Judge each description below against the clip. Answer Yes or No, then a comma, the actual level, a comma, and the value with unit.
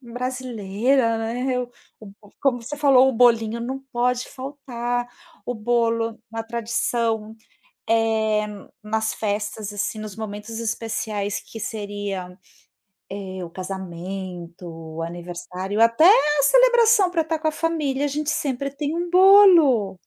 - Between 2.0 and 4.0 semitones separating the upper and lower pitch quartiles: No, average, 4.6 semitones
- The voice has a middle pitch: No, high, 230 Hz